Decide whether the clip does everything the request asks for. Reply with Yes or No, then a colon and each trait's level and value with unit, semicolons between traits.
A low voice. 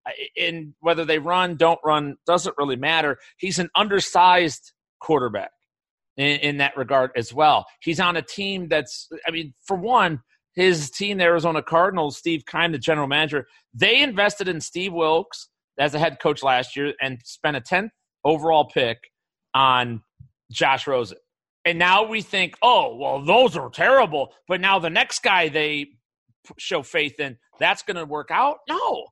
No: medium, 160 Hz